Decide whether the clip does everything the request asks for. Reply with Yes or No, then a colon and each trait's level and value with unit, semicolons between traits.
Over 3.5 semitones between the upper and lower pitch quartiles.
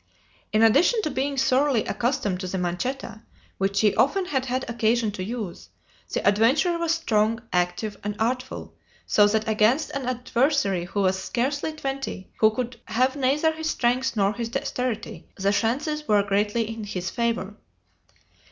Yes: average, 4.5 semitones